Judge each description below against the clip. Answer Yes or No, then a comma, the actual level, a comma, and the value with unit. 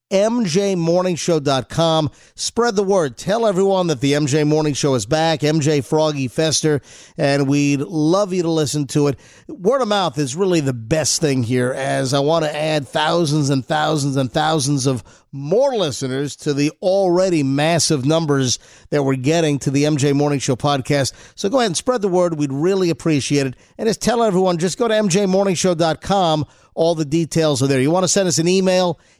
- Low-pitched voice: No, medium, 155 Hz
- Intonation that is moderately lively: Yes, average, 4.0 semitones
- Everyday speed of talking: Yes, average, 190 wpm